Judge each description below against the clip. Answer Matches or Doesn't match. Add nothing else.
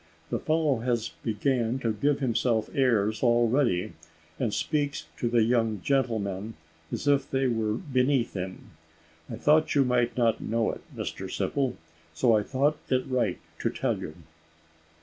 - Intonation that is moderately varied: Matches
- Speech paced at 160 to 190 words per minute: Doesn't match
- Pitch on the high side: Doesn't match